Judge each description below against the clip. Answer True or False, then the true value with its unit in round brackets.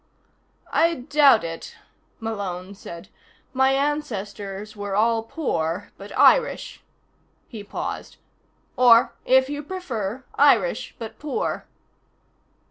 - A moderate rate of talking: False (100 wpm)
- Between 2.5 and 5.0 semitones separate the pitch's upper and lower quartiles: False (5.4 semitones)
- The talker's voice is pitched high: True (225 Hz)